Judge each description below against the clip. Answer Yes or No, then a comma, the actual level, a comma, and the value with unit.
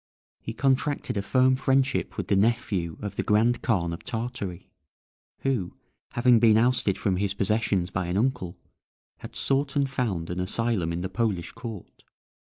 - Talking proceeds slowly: No, average, 160 wpm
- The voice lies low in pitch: Yes, low, 110 Hz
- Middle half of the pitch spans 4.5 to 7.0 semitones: Yes, average, 5.2 semitones